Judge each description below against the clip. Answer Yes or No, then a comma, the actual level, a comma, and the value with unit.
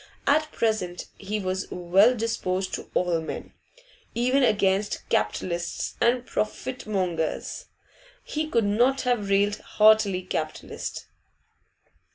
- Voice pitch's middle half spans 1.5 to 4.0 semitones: No, average, 4.4 semitones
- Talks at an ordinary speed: No, slow, 105 wpm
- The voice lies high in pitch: Yes, high, 205 Hz